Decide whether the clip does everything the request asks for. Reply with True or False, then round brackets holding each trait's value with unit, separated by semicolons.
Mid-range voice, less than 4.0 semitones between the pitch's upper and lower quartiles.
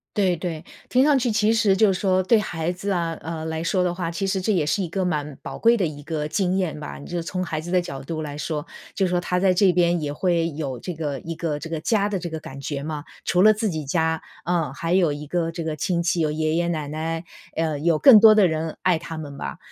True (170 Hz; 3.0 semitones)